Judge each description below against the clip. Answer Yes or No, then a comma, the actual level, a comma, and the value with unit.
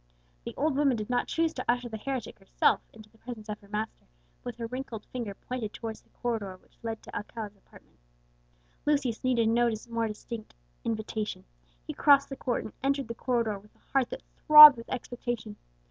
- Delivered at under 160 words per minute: No, average, 195 wpm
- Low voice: No, high, 230 Hz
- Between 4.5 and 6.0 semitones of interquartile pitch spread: No, average, 2.9 semitones